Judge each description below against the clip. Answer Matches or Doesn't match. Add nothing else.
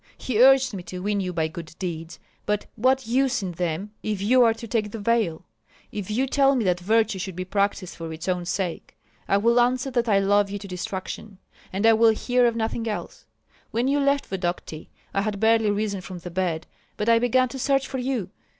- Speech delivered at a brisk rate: Matches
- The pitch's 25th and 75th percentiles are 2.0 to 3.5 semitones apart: Doesn't match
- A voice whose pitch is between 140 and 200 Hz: Doesn't match